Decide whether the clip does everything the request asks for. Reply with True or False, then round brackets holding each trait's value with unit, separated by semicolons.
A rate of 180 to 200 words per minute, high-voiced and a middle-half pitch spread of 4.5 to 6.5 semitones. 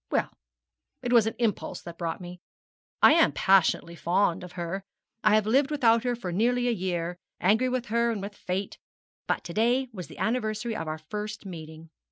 True (195 wpm; 210 Hz; 5.0 semitones)